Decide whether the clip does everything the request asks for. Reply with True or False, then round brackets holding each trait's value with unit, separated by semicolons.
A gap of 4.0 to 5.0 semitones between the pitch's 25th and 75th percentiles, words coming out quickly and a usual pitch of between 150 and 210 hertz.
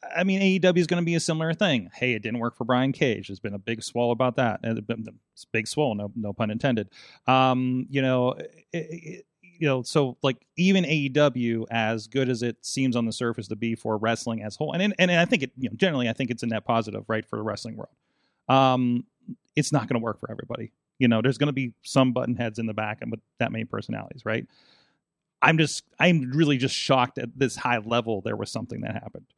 False (4.5 semitones; 240 wpm; 125 Hz)